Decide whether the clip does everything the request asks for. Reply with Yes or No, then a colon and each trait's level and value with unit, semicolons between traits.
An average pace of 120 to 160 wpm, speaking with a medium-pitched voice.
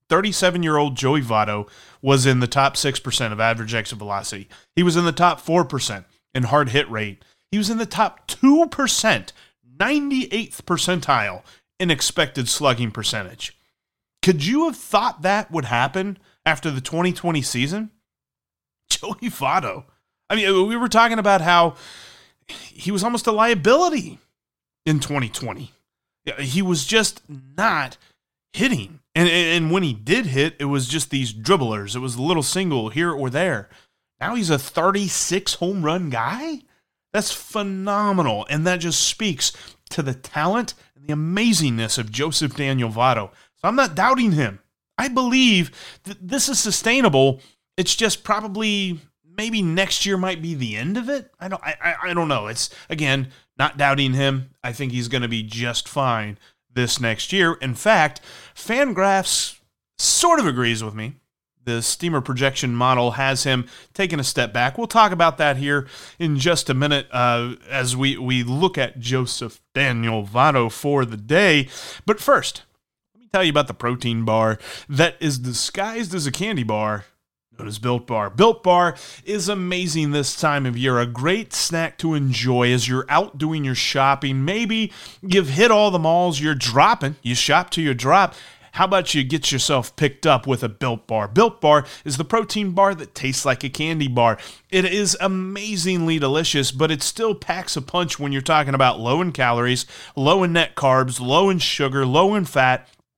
No: average, 175 wpm; medium, 150 Hz